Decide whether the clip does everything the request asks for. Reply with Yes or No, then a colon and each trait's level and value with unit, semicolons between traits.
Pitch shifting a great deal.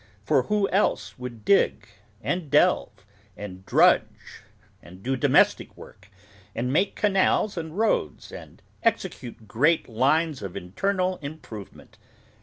Yes: wide, 9.0 semitones